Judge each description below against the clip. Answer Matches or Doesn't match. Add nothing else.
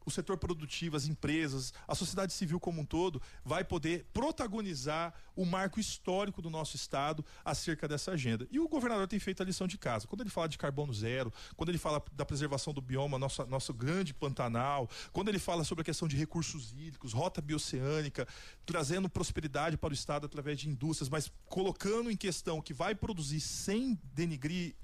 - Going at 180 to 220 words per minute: Matches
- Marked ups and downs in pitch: Doesn't match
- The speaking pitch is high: Doesn't match